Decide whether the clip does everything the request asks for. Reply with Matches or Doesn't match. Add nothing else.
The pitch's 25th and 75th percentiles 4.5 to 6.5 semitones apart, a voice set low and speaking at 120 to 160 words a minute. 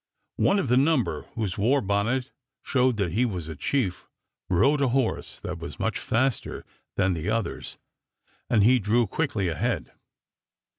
Matches